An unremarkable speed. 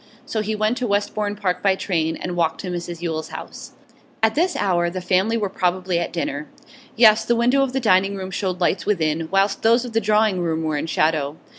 No: fast, 220 wpm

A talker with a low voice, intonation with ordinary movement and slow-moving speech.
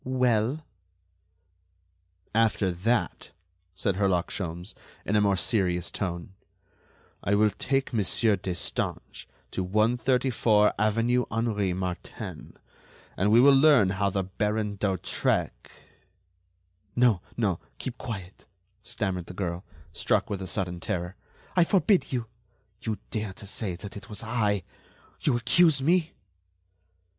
Yes: low, 105 Hz; average, 4.1 semitones; slow, 120 wpm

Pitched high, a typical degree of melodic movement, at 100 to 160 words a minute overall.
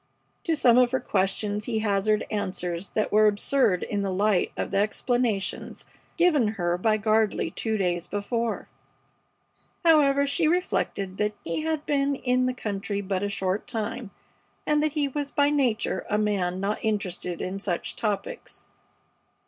Yes: high, 215 Hz; average, 4.7 semitones; average, 155 wpm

